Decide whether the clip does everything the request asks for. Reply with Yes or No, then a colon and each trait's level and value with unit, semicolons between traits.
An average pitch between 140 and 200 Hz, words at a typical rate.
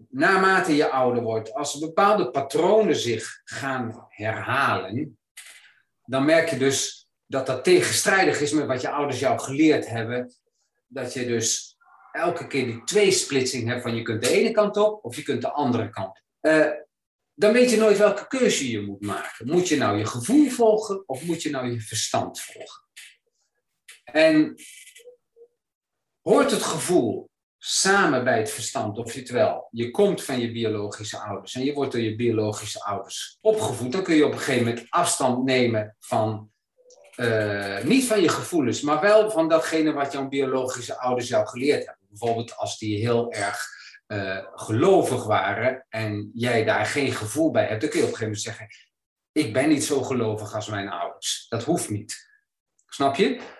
No: low, 130 Hz; average, 180 wpm